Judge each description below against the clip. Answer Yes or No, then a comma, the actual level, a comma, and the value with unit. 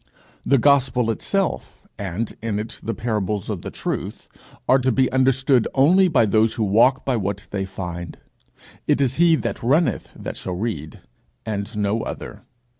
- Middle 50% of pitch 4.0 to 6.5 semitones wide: Yes, average, 4.6 semitones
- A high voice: No, low, 115 Hz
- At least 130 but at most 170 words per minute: Yes, average, 165 wpm